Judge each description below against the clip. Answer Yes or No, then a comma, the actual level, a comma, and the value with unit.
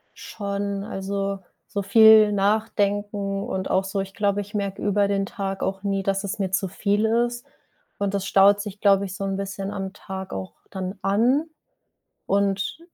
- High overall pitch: Yes, high, 200 Hz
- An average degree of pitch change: No, narrow, 1.0 semitones